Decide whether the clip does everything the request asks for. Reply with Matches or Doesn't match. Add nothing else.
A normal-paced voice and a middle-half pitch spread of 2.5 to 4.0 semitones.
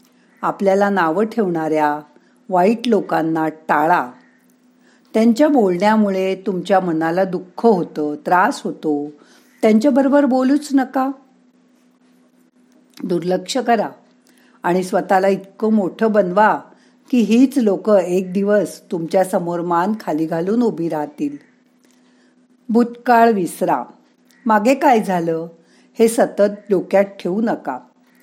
Doesn't match